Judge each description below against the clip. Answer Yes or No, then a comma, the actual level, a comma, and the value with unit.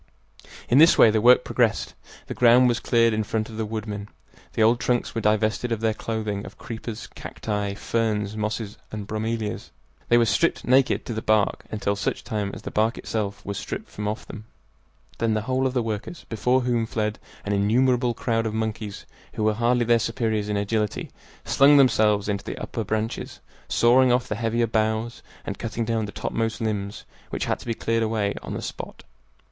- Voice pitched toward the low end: Yes, low, 110 Hz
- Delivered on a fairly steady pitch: Yes, narrow, 1.8 semitones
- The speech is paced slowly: No, average, 195 wpm